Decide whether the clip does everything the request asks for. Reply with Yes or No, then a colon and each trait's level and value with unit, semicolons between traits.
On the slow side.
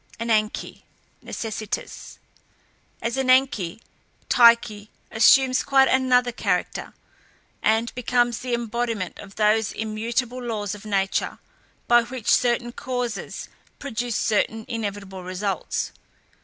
Yes: slow, 100 wpm